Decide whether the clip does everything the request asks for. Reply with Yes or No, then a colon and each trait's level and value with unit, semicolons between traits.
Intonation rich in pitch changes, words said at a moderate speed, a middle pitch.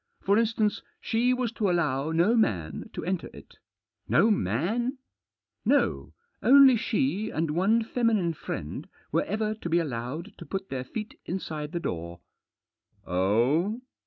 Yes: wide, 8.4 semitones; average, 155 wpm; medium, 180 Hz